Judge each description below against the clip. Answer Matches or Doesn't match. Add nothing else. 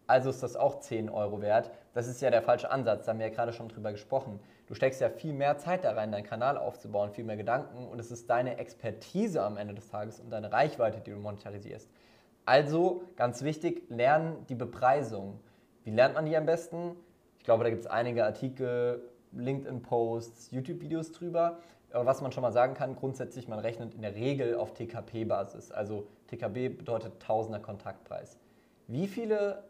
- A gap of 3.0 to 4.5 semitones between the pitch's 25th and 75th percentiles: Matches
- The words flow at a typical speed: Doesn't match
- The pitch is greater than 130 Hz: Doesn't match